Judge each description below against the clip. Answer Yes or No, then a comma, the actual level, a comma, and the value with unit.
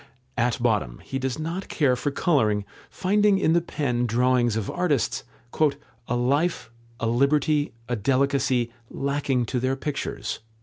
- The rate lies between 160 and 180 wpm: No, average, 140 wpm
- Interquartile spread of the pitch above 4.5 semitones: No, average, 3.7 semitones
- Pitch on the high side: No, low, 130 Hz